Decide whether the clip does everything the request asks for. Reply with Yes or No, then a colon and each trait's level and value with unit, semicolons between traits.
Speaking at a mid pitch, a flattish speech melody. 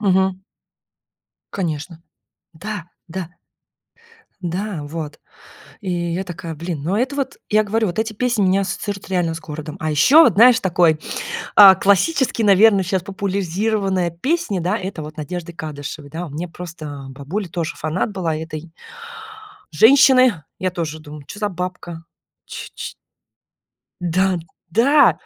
No: medium, 180 Hz; average, 3.9 semitones